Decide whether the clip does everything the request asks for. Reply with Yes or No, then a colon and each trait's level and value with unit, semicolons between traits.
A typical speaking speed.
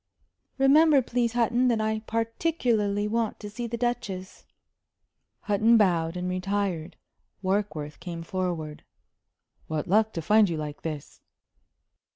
No: slow, 125 wpm